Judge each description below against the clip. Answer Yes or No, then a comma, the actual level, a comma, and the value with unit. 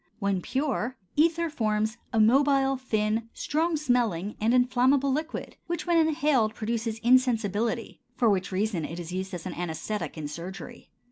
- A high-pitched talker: Yes, high, 230 Hz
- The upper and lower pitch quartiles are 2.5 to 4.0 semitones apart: No, average, 4.9 semitones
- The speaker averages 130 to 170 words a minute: Yes, average, 150 wpm